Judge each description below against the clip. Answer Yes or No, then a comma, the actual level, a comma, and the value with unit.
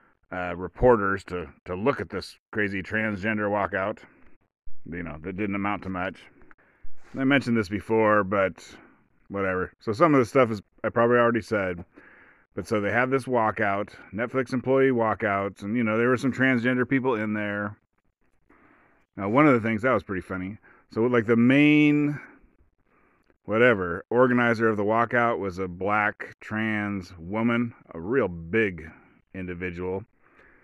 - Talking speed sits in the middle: Yes, average, 155 wpm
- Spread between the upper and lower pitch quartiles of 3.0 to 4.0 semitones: Yes, average, 3.6 semitones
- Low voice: Yes, low, 110 Hz